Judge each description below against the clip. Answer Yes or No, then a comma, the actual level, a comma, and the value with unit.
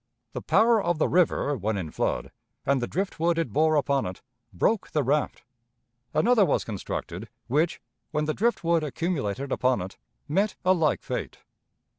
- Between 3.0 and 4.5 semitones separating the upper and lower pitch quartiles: No, average, 5.2 semitones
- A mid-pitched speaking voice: Yes, medium, 155 Hz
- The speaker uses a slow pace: No, average, 170 wpm